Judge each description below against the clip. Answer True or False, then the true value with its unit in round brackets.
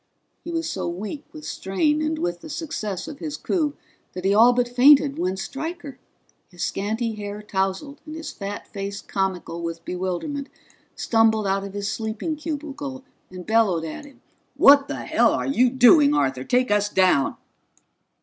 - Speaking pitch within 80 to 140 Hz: False (225 Hz)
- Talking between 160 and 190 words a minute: True (170 wpm)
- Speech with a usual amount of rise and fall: False (7.0 semitones)